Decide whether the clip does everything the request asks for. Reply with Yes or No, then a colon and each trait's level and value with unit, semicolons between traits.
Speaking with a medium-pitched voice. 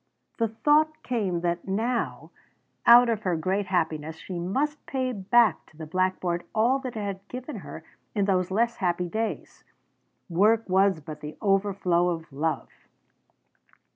No: high, 195 Hz